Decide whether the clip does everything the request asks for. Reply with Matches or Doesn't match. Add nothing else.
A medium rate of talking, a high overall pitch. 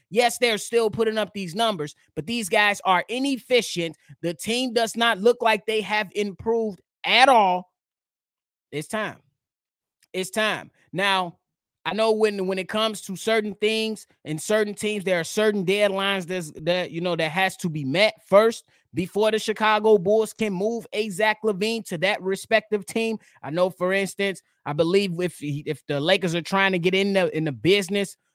Matches